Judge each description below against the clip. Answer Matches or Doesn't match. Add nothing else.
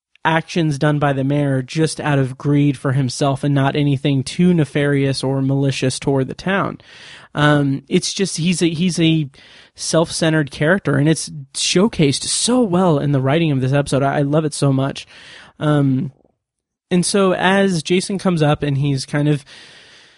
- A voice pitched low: Doesn't match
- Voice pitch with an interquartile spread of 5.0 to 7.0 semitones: Doesn't match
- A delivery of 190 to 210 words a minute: Doesn't match